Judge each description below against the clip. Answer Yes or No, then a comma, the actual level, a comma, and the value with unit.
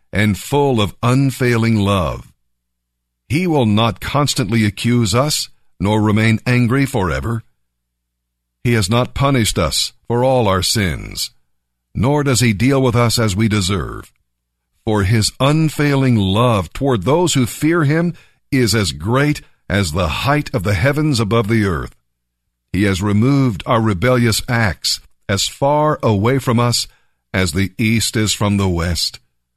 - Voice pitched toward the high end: No, low, 110 Hz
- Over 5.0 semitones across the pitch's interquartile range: Yes, wide, 5.5 semitones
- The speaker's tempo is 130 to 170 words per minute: Yes, average, 145 wpm